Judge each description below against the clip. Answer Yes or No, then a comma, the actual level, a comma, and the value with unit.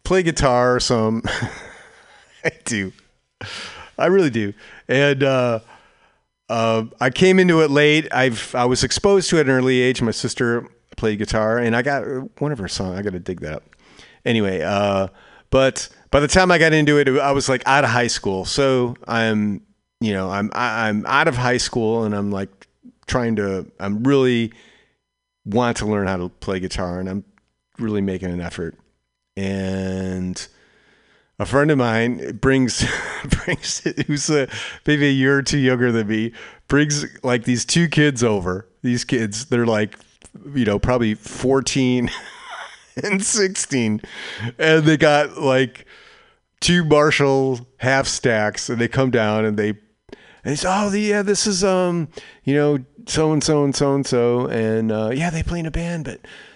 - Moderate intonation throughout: Yes, average, 5.0 semitones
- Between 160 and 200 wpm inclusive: Yes, average, 170 wpm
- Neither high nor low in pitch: No, low, 125 Hz